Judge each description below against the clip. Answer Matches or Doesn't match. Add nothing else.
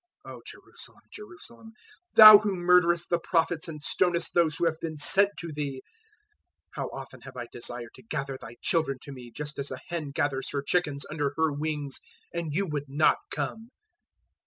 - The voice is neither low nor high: Matches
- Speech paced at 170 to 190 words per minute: Matches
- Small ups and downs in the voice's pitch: Doesn't match